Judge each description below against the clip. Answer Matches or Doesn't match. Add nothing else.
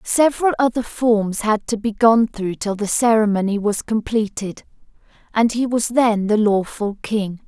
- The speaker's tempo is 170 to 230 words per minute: Doesn't match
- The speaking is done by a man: Doesn't match